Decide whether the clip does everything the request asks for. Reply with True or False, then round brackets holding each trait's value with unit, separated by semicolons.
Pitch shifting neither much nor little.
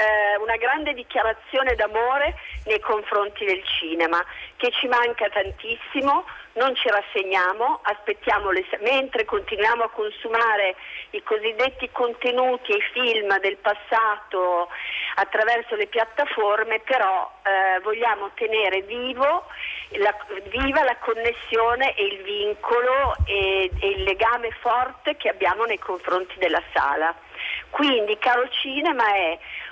True (4.5 semitones)